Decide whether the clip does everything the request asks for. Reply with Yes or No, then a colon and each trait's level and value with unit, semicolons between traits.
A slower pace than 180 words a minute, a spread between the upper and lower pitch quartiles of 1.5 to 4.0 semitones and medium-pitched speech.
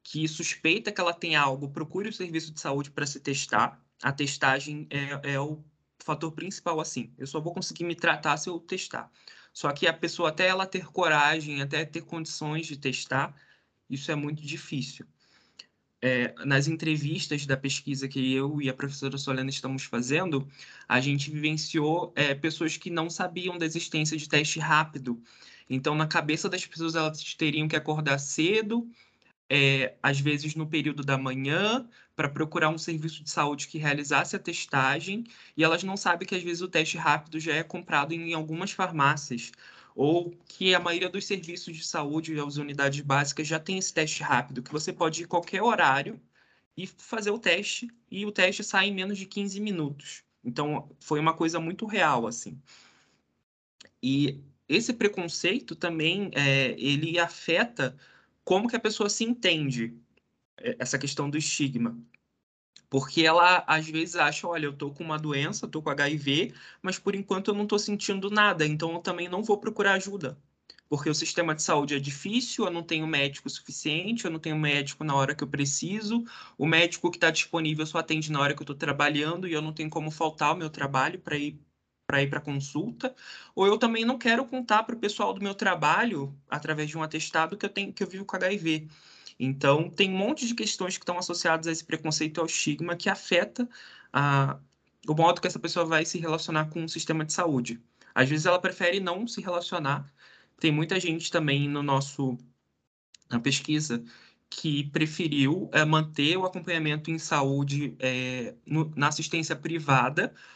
No: fast, 185 wpm; average, 3.6 semitones; medium, 155 Hz